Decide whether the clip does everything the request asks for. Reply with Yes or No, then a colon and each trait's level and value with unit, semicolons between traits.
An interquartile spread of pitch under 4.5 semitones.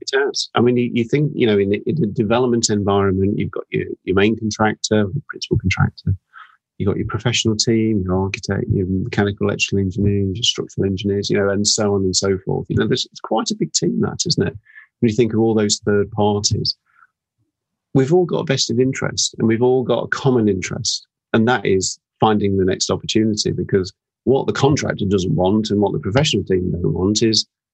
Yes: average, 3.0 semitones